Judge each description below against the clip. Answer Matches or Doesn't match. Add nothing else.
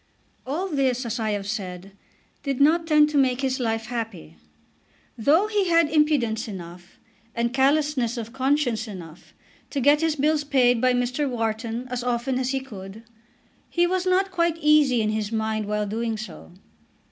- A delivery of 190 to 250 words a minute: Doesn't match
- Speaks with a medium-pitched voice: Doesn't match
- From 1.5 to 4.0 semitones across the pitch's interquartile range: Doesn't match